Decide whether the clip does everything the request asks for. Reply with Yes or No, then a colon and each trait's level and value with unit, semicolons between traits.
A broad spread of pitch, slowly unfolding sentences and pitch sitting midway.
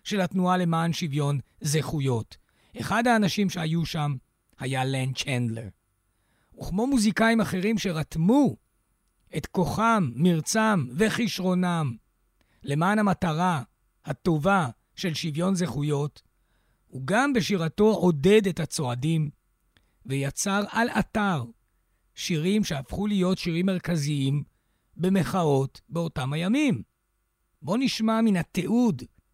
Yes: wide, 6.6 semitones; slow, 95 wpm; medium, 165 Hz